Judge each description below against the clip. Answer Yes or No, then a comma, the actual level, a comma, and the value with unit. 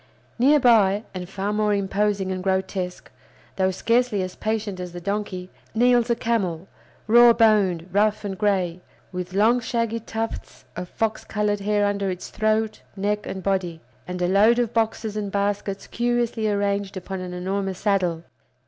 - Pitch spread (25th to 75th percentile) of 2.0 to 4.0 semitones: Yes, narrow, 2.6 semitones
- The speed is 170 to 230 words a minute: No, average, 160 wpm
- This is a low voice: No, high, 205 Hz